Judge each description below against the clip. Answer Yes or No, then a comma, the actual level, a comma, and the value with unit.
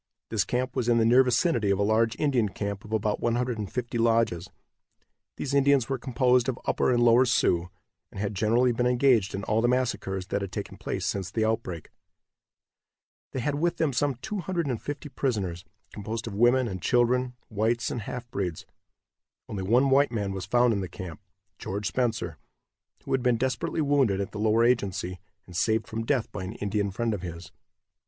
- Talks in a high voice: No, low, 115 Hz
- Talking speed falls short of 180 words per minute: No, average, 185 wpm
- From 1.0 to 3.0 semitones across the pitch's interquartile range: No, average, 3.9 semitones